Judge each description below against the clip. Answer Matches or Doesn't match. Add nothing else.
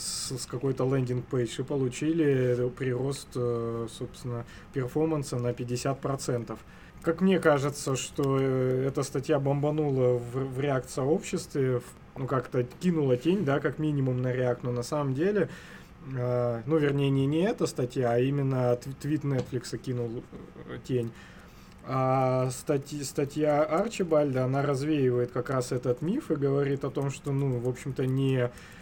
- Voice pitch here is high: Doesn't match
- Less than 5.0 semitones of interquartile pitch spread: Matches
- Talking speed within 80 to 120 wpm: Doesn't match